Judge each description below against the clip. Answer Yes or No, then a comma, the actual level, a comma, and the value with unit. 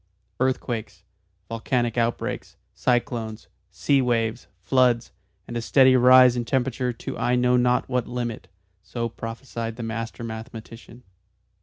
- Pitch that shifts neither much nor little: No, narrow, 1.6 semitones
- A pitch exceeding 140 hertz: No, low, 120 Hz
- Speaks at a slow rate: Yes, slow, 125 wpm